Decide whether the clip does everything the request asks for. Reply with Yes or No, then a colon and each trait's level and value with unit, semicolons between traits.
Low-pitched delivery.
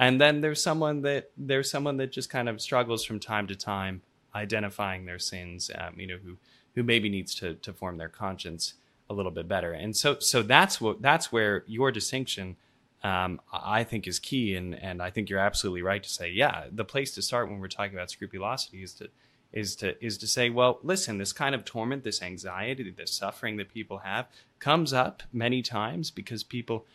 Yes: low, 110 Hz